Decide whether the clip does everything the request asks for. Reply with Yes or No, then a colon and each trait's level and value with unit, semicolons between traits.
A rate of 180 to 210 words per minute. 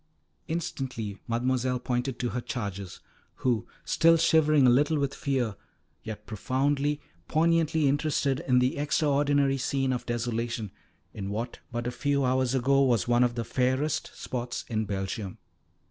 No: average, 145 wpm